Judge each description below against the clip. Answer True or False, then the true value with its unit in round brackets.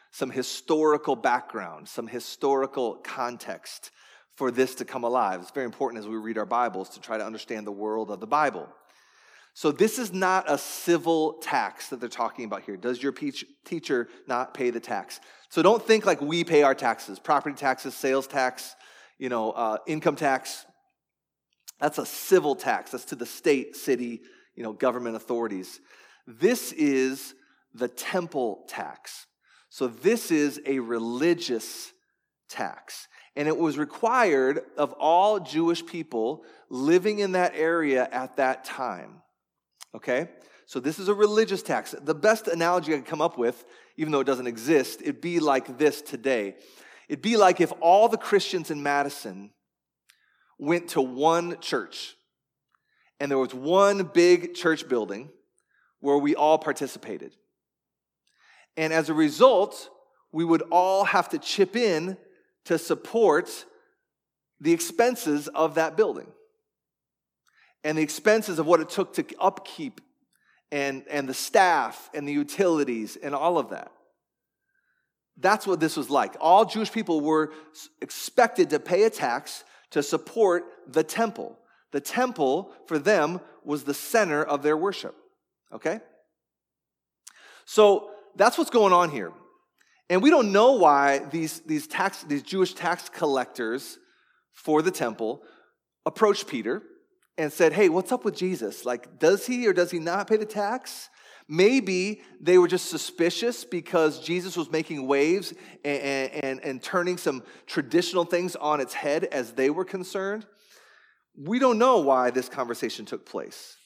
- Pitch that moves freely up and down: True (6.8 semitones)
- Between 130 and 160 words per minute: True (155 wpm)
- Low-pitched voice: False (165 Hz)